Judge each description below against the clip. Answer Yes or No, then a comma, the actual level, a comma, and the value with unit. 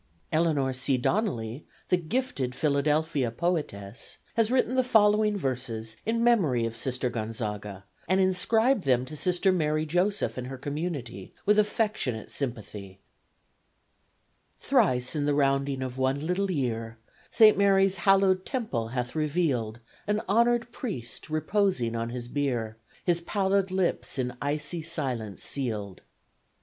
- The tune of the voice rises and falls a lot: Yes, wide, 7.7 semitones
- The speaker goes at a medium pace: No, slow, 130 wpm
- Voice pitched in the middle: Yes, medium, 145 Hz